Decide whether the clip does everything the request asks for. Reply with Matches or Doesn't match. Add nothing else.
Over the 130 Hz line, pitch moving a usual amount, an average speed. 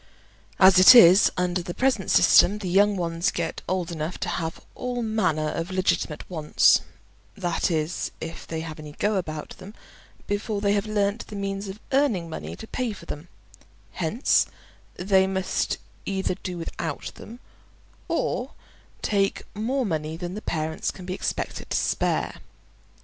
Matches